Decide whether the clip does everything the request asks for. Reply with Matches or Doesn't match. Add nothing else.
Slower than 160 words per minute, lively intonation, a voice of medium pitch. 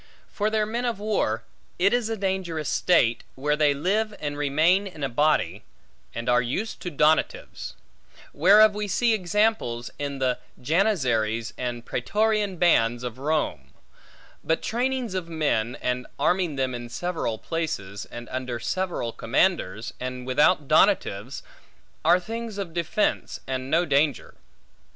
Matches